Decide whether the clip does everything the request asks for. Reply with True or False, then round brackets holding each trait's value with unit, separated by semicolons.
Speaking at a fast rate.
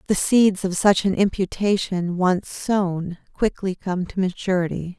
False (145 wpm)